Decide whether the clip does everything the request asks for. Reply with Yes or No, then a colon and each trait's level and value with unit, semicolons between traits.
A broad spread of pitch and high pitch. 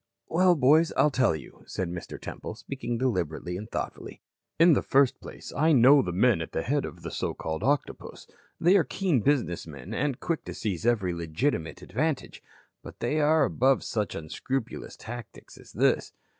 No: wide, 8.5 semitones; low, 130 Hz